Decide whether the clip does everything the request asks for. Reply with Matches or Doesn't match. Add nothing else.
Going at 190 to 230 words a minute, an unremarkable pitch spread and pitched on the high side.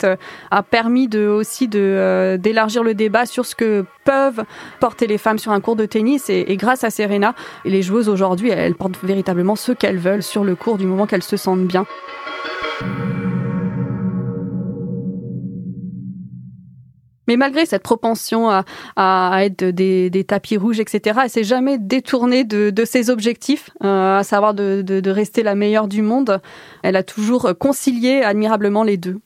Doesn't match